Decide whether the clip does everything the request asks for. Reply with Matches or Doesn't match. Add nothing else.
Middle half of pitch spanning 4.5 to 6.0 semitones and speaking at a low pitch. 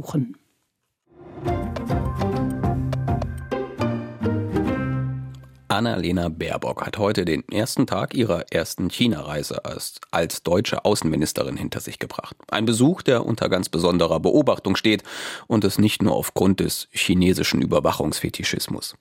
Matches